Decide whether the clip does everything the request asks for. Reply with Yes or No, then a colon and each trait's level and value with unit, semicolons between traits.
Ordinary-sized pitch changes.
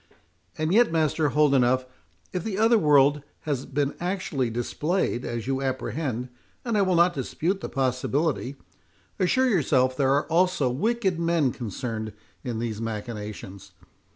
No: wide, 5.7 semitones